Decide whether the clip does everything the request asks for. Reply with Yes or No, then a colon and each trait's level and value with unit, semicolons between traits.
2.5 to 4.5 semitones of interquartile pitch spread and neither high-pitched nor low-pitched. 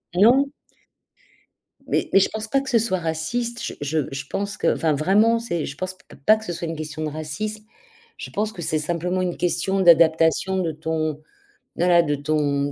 No: average, 5.1 semitones; medium, 175 Hz